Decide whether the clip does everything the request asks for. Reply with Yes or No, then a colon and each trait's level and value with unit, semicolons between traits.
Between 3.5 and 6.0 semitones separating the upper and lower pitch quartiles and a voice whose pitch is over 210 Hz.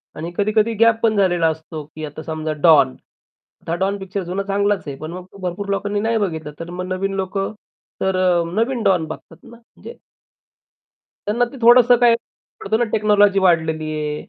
No: average, 4.4 semitones; high, 190 Hz